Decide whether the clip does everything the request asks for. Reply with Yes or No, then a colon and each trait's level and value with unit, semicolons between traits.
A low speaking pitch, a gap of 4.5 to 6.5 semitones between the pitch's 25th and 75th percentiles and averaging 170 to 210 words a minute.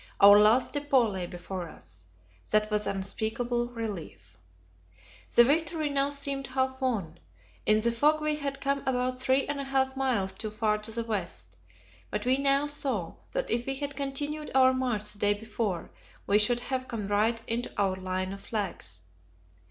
No: high, 235 Hz; average, 4.8 semitones; average, 175 wpm